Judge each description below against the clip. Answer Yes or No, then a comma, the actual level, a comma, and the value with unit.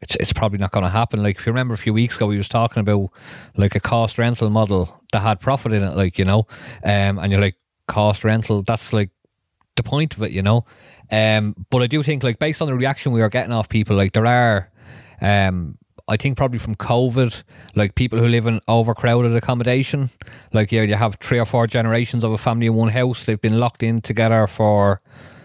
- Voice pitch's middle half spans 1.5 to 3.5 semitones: Yes, narrow, 2.5 semitones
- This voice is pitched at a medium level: No, low, 115 Hz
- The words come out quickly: Yes, fast, 230 wpm